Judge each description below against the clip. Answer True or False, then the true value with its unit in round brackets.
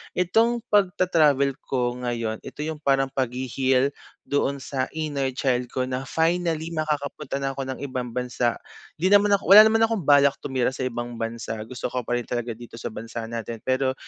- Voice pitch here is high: False (135 Hz)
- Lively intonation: False (4.1 semitones)